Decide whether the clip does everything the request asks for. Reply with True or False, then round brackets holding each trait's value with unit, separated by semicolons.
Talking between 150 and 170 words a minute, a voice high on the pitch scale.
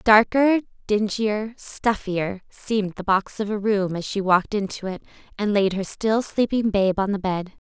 False (180 wpm; 205 Hz)